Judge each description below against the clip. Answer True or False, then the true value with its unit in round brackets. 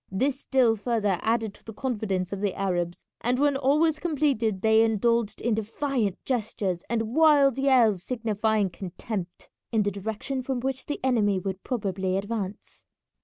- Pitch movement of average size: True (4.7 semitones)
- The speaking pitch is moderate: False (220 Hz)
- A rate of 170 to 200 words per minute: False (160 wpm)